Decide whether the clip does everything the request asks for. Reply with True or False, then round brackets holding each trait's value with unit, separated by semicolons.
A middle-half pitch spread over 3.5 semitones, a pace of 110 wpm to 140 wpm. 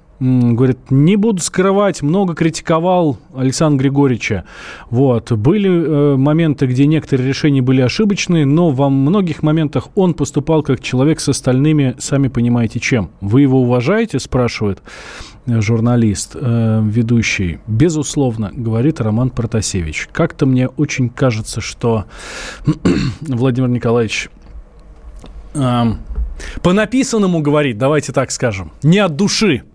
True (4.7 semitones; 120 wpm)